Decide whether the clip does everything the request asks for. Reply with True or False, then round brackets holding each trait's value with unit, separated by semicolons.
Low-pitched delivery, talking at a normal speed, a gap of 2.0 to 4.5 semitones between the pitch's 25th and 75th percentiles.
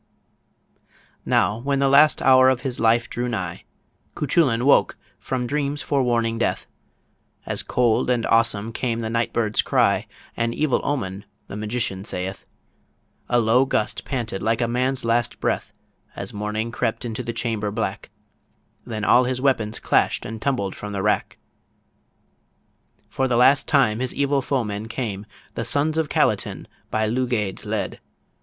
True (120 Hz; 150 wpm; 3.1 semitones)